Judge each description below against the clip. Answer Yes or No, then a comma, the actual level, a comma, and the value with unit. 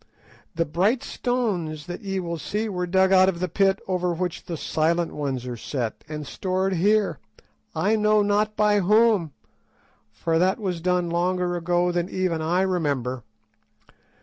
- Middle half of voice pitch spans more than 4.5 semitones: No, average, 2.8 semitones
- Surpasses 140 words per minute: Yes, average, 160 wpm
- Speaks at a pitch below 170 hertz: No, medium, 180 Hz